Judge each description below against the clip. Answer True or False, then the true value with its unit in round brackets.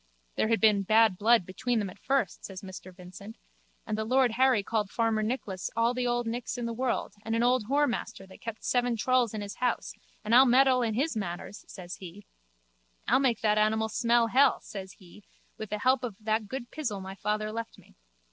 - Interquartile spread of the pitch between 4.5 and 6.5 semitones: False (2.9 semitones)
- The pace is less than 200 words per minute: False (205 wpm)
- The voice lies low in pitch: False (225 Hz)